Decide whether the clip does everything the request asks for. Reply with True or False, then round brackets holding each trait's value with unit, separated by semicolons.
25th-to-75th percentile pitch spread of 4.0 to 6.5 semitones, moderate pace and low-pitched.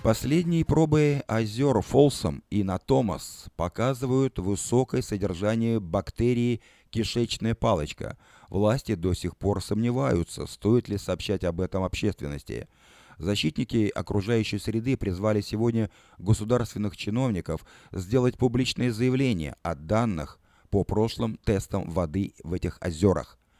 False (4.3 semitones; 105 wpm; 105 Hz)